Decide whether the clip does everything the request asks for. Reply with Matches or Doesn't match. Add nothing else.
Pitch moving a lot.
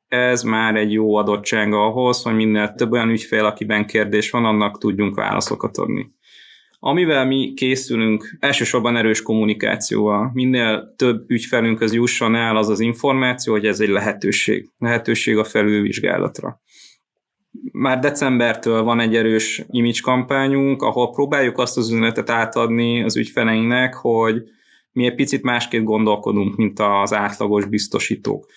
Doesn't match